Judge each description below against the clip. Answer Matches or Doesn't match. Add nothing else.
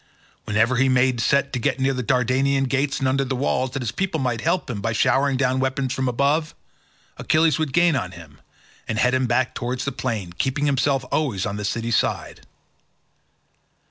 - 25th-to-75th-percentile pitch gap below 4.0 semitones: Matches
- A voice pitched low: Matches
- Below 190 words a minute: Doesn't match